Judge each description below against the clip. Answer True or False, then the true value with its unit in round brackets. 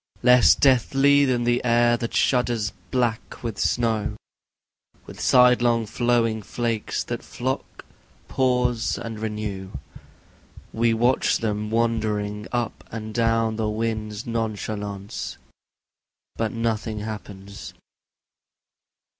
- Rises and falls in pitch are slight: True (2.0 semitones)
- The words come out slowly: True (100 wpm)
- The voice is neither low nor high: False (115 Hz)